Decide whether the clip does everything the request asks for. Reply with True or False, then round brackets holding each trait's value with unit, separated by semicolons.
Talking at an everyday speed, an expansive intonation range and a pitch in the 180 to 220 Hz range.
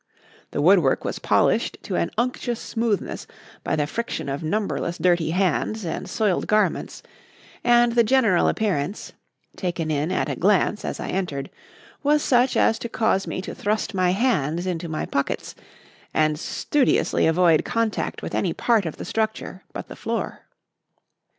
True (155 wpm; 5.7 semitones; 190 Hz)